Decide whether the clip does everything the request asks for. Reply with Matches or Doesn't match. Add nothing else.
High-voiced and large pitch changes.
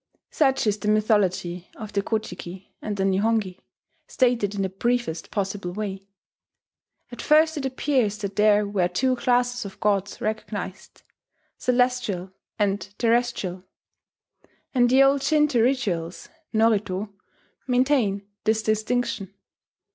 Doesn't match